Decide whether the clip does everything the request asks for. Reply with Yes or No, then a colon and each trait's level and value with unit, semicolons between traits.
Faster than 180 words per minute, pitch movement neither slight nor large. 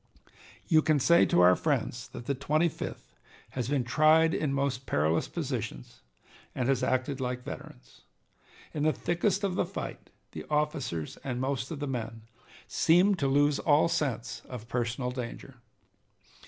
No: average, 155 wpm; average, 3.9 semitones